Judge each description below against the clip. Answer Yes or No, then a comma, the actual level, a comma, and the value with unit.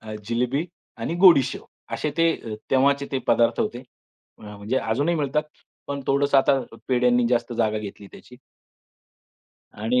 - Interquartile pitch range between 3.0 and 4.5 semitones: Yes, average, 3.3 semitones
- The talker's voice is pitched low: Yes, low, 125 Hz